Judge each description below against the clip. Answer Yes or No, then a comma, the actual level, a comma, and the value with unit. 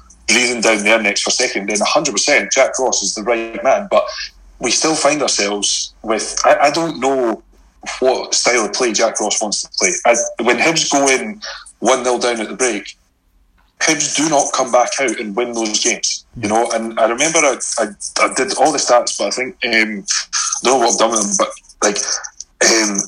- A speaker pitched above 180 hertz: No, low, 115 Hz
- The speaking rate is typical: No, fast, 210 wpm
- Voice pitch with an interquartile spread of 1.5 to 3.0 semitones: No, average, 4.1 semitones